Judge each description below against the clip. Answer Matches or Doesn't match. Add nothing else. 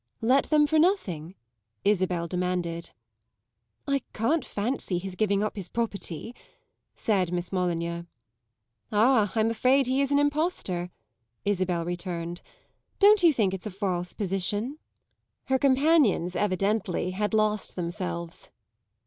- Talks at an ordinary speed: Doesn't match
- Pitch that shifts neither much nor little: Doesn't match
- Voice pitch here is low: Doesn't match